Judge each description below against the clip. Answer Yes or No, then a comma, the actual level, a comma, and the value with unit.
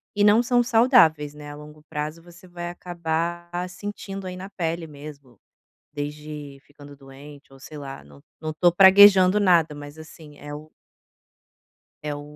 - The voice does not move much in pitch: No, average, 3.7 semitones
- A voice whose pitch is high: No, medium, 155 Hz